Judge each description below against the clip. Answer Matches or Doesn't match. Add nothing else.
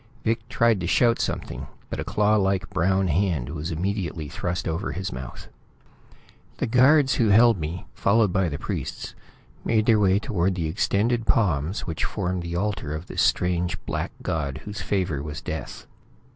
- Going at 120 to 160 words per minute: Doesn't match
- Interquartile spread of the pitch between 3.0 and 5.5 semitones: Matches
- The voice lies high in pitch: Doesn't match